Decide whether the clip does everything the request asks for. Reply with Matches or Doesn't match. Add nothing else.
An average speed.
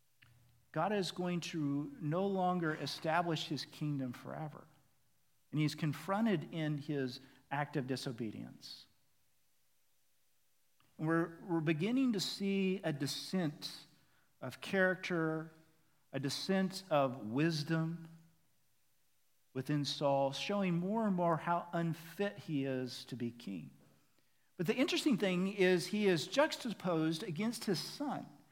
Doesn't match